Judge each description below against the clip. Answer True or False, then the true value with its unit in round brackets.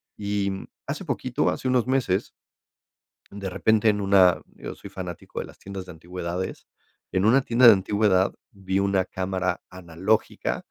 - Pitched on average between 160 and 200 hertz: False (95 Hz)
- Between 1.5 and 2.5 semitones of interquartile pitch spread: True (2.1 semitones)